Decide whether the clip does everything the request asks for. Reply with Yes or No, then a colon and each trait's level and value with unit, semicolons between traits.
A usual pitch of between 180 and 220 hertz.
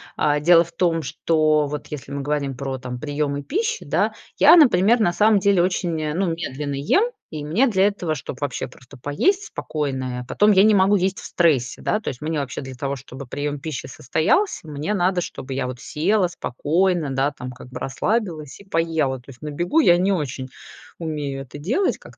No: medium, 155 Hz